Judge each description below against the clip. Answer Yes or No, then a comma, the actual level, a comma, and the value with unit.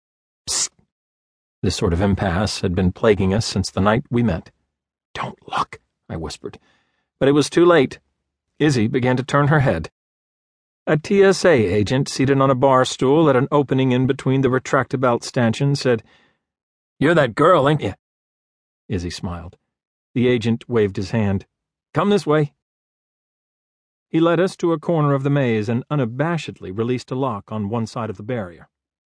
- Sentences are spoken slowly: No, average, 165 wpm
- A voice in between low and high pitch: No, low, 120 Hz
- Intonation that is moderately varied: No, wide, 6.5 semitones